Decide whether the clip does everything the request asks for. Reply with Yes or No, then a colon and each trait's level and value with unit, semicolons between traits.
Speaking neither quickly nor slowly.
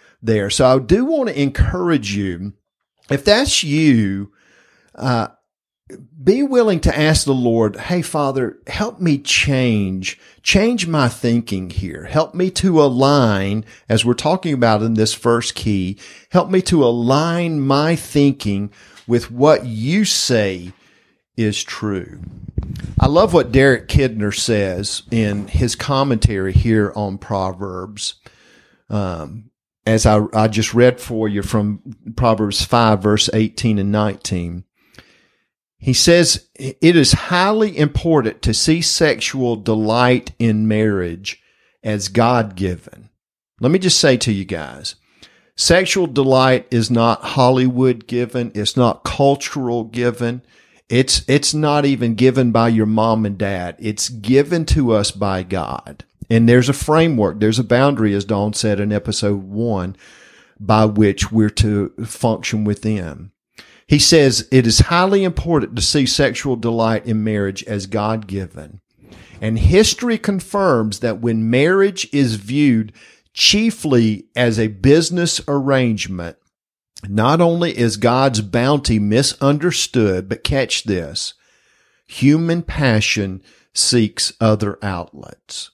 No: slow, 130 wpm